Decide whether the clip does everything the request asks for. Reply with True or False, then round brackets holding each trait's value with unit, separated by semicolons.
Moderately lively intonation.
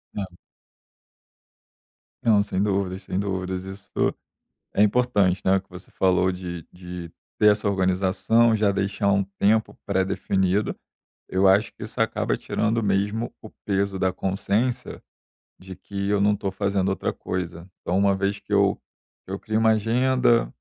False (1.7 semitones)